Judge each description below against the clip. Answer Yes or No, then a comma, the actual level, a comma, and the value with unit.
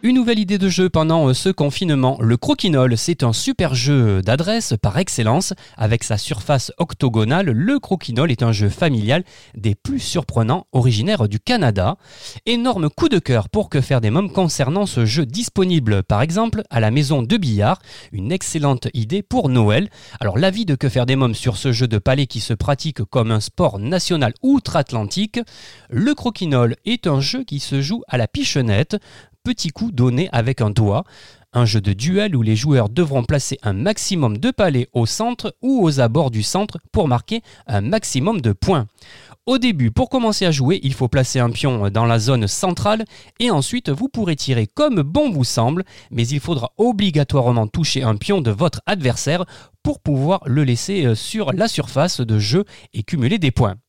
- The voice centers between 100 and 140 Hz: Yes, low, 135 Hz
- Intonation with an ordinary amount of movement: No, wide, 7.8 semitones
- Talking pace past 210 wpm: No, average, 185 wpm